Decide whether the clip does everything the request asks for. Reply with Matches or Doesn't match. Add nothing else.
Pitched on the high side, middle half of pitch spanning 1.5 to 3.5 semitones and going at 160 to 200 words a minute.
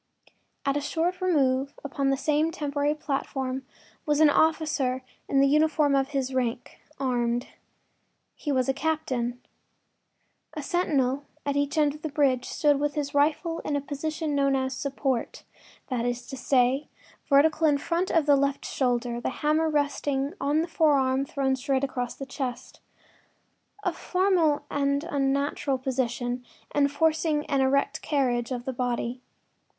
Doesn't match